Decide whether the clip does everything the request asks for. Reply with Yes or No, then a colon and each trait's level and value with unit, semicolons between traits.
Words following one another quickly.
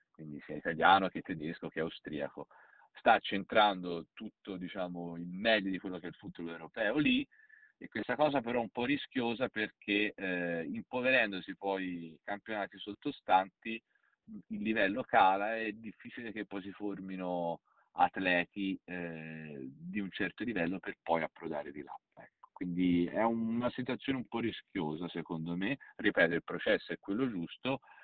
No: average, 155 wpm